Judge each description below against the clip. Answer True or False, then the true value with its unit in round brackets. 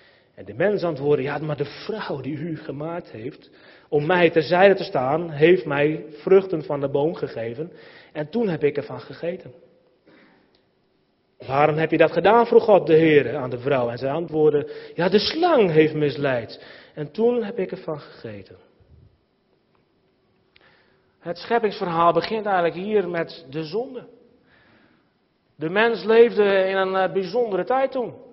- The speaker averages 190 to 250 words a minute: False (150 wpm)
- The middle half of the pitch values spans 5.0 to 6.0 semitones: True (5.3 semitones)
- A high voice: False (170 Hz)